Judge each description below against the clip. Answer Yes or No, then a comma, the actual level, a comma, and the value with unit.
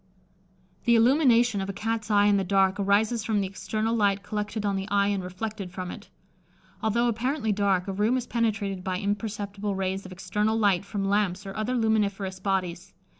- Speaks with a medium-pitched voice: No, high, 205 Hz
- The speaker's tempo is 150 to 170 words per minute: No, average, 185 wpm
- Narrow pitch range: Yes, narrow, 2.2 semitones